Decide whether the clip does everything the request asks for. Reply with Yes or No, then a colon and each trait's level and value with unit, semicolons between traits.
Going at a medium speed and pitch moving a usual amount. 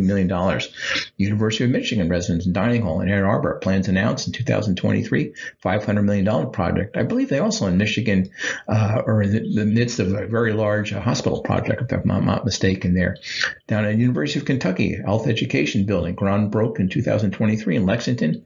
No: average, 185 wpm; narrow, 2.3 semitones